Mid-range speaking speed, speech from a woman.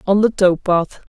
No: fast, 215 wpm; female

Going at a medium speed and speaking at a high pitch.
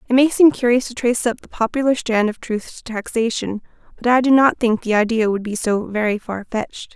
No: fast, 235 wpm; high, 230 Hz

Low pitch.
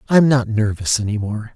Yes: low, 115 Hz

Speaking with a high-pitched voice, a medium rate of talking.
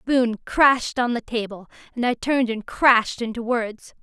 Yes: high, 235 Hz; average, 195 wpm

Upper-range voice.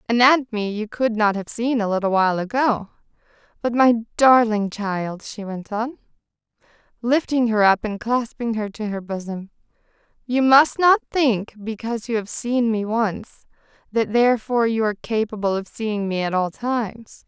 Yes: high, 220 Hz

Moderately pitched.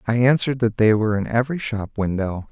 No: low, 115 Hz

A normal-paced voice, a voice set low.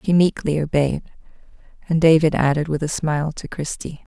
No: average, 160 wpm; medium, 155 Hz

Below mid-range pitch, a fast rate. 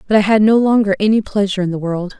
No: high, 205 Hz; fast, 275 wpm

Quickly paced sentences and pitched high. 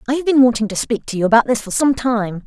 Yes: fast, 315 wpm; high, 240 Hz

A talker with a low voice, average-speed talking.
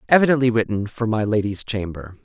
Yes: low, 110 Hz; average, 160 wpm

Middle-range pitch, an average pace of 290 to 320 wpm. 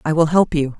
Yes: medium, 155 Hz; fast, 305 wpm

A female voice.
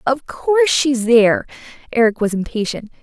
Yes: female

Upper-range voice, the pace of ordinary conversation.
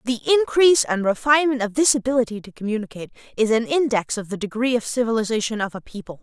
Yes: high, 235 Hz; average, 195 wpm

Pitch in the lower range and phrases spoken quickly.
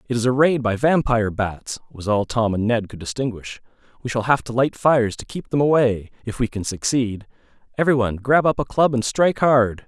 Yes: low, 120 Hz; fast, 225 wpm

